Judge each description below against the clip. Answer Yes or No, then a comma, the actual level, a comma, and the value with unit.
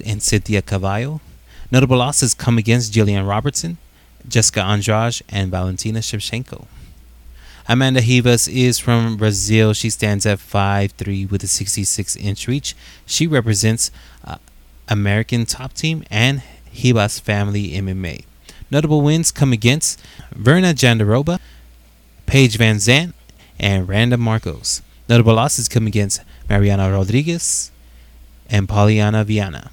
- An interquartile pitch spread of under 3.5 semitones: No, average, 4.0 semitones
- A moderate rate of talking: No, slow, 120 wpm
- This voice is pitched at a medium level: No, low, 110 Hz